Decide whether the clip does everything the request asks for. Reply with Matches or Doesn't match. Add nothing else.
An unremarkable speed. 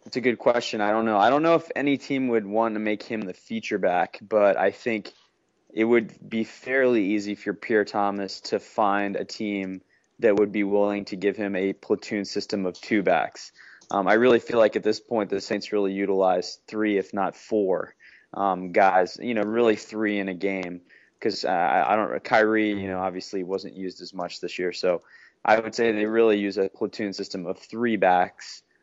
Doesn't match